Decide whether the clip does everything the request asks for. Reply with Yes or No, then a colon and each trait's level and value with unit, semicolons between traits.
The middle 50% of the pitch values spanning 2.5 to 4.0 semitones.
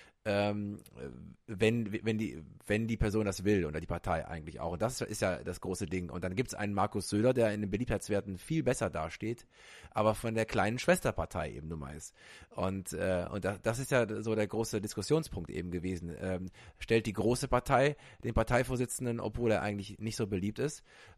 Yes: average, 3.5 semitones